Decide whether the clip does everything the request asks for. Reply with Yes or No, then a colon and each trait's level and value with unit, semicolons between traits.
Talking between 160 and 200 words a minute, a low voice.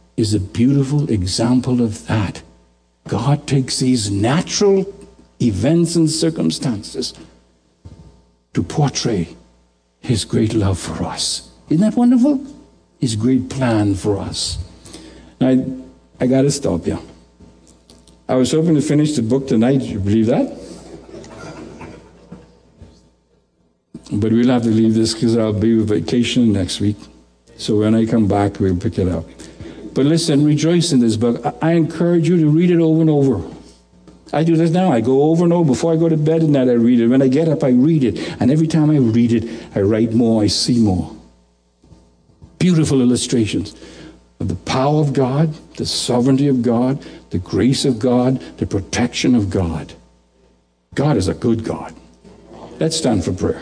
Yes: average, 170 wpm; low, 115 Hz